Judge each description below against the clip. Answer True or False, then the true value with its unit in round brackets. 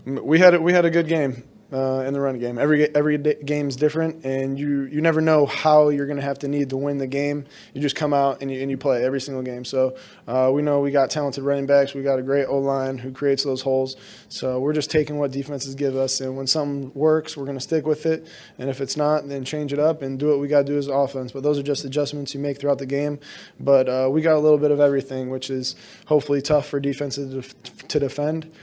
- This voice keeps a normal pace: False (265 wpm)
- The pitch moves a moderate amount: False (1.7 semitones)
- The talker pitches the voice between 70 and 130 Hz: False (140 Hz)